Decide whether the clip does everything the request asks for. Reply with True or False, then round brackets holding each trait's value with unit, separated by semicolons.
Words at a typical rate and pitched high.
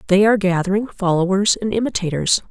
True (145 wpm; 195 Hz)